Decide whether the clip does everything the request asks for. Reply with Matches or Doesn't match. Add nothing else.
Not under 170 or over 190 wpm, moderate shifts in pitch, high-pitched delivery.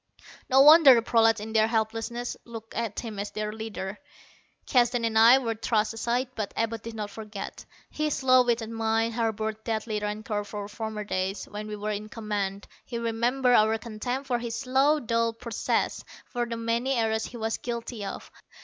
Doesn't match